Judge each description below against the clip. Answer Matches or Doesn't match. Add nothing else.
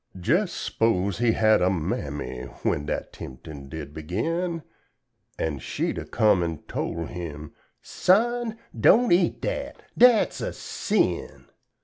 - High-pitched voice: Doesn't match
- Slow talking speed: Matches